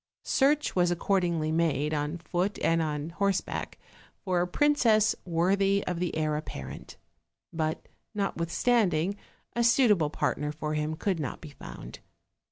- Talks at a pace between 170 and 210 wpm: No, average, 140 wpm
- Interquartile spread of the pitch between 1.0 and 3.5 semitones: No, average, 4.2 semitones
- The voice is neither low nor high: Yes, medium, 175 Hz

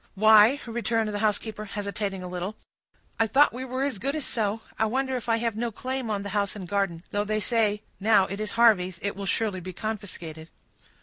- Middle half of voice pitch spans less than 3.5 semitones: Yes, narrow, 2.5 semitones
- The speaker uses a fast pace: Yes, fast, 210 wpm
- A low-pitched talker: No, high, 215 Hz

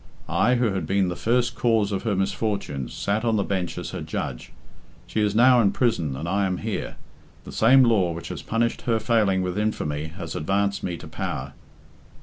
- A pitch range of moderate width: Yes, average, 3.7 semitones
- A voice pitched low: Yes, low, 100 Hz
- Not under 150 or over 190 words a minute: No, average, 200 wpm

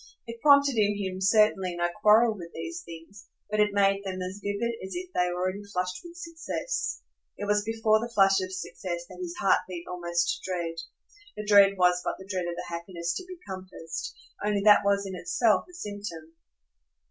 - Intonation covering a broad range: No, average, 2.9 semitones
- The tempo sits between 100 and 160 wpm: No, average, 195 wpm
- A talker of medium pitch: No, high, 195 Hz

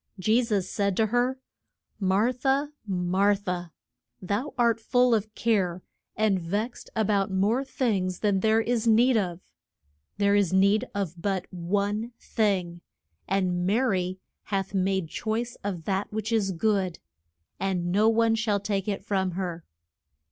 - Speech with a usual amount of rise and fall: Yes, average, 3.0 semitones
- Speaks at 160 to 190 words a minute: No, average, 150 wpm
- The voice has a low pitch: No, high, 200 Hz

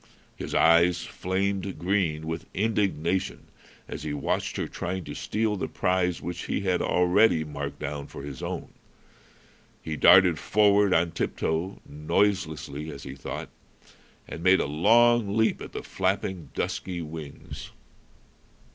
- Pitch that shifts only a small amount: No, average, 3.9 semitones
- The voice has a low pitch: Yes, very low, 90 Hz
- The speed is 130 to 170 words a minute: Yes, average, 140 wpm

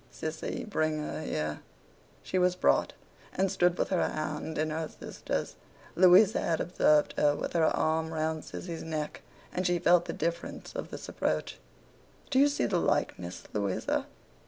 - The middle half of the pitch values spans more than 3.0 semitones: No, narrow, 2.5 semitones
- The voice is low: No, medium, 160 Hz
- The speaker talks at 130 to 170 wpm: Yes, average, 160 wpm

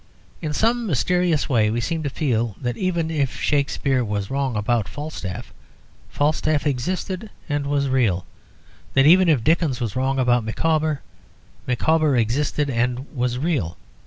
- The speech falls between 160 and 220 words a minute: No, average, 145 wpm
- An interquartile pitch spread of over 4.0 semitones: Yes, average, 4.4 semitones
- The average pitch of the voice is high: No, medium, 140 Hz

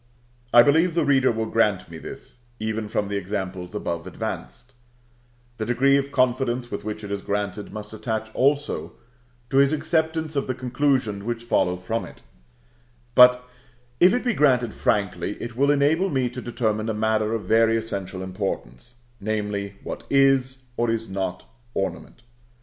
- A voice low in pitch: Yes, low, 115 Hz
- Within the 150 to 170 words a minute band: Yes, average, 165 wpm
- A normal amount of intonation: Yes, average, 4.6 semitones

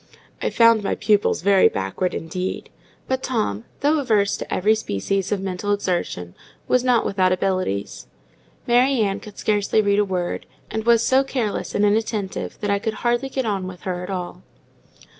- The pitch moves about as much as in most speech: Yes, average, 3.7 semitones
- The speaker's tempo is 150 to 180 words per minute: Yes, average, 175 wpm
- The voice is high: Yes, high, 205 Hz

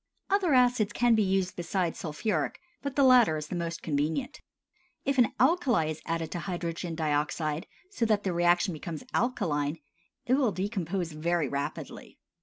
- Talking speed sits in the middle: Yes, average, 160 wpm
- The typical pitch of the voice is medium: Yes, medium, 175 Hz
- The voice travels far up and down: Yes, wide, 6.8 semitones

